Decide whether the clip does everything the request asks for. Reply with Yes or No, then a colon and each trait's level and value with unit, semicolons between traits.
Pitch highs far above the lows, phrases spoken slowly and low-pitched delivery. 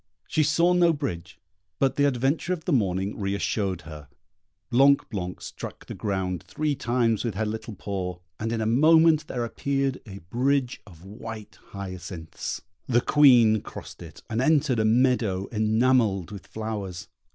No: wide, 5.8 semitones; average, 160 wpm; low, 110 Hz